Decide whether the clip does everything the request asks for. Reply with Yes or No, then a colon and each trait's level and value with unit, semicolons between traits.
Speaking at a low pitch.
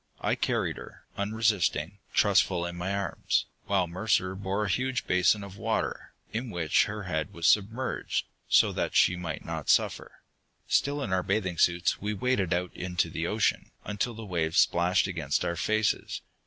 Yes: very low, 95 Hz